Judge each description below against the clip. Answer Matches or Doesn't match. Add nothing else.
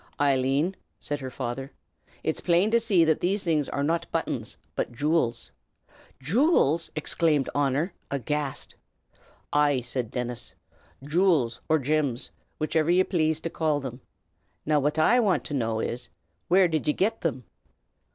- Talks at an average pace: Matches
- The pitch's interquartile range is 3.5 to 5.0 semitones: Matches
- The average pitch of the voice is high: Doesn't match